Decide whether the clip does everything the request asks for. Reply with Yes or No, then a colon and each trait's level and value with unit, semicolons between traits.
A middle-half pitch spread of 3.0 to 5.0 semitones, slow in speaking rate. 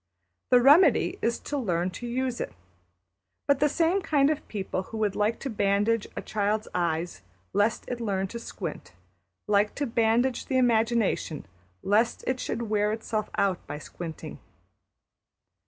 No: average, 3.7 semitones; average, 155 wpm